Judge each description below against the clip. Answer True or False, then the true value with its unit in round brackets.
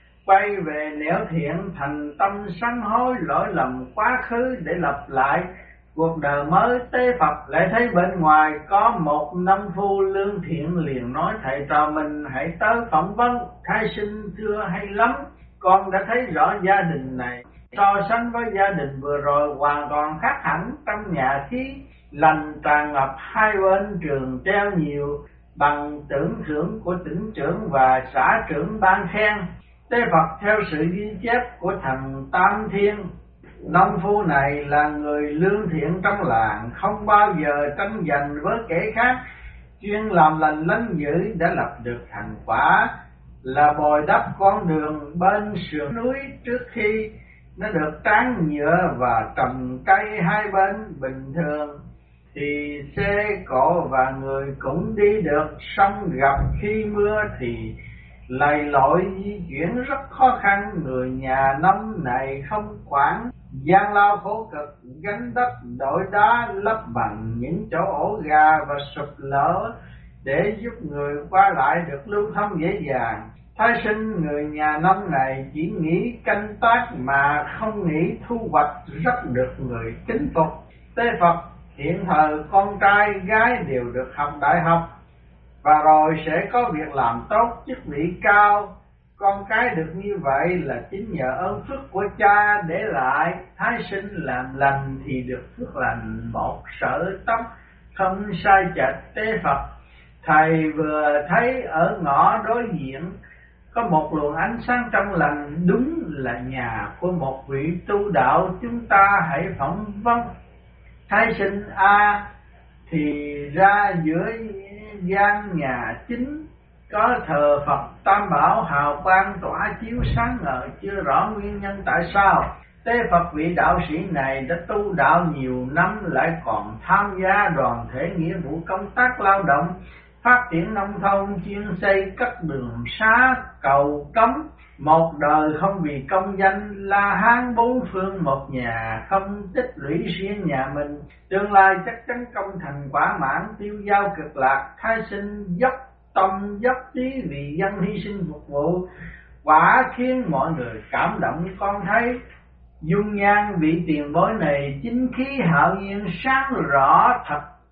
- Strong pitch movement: True (5.8 semitones)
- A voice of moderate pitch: True (180 Hz)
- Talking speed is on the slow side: True (160 wpm)